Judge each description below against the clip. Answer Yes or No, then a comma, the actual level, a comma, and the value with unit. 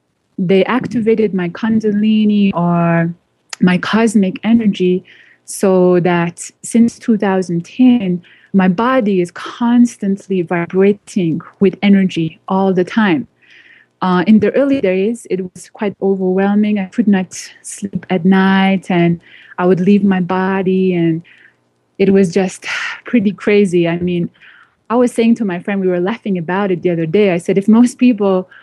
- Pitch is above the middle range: Yes, high, 195 Hz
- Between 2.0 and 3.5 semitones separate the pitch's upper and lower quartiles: Yes, average, 3.1 semitones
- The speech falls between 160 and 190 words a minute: No, average, 145 wpm